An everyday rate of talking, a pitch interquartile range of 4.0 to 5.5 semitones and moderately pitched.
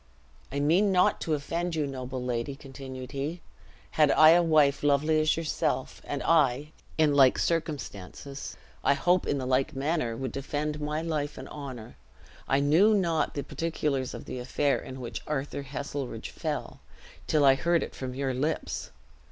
No: average, 170 wpm; average, 2.8 semitones; medium, 145 Hz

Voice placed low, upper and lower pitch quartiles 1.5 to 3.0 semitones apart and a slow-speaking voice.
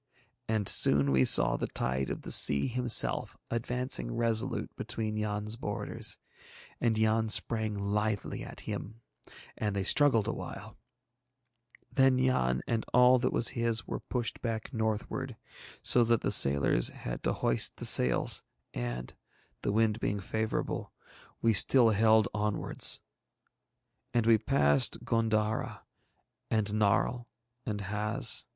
Yes: low, 110 Hz; narrow, 2.5 semitones; slow, 130 wpm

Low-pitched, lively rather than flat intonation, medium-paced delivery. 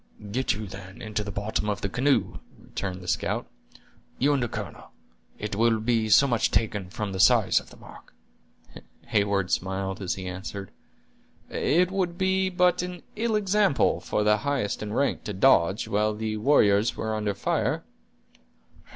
Yes: low, 110 Hz; wide, 5.8 semitones; average, 170 wpm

